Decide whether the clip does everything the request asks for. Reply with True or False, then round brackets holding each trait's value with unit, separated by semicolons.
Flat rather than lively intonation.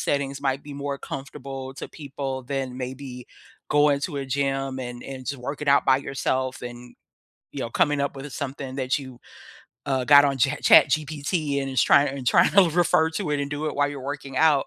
True (1.5 semitones)